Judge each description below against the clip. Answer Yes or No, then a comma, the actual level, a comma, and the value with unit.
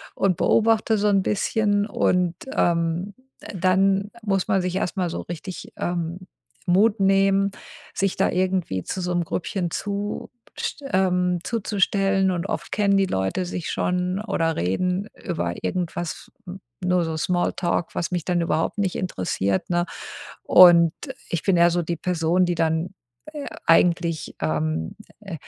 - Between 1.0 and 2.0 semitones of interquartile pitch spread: No, narrow, 2.5 semitones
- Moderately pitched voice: Yes, medium, 180 Hz